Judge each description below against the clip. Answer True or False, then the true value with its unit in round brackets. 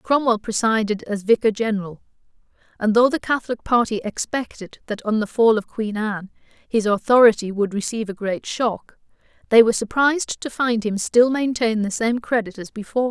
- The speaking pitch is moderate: False (225 Hz)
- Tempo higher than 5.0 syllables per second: True (5.4 syllables/s)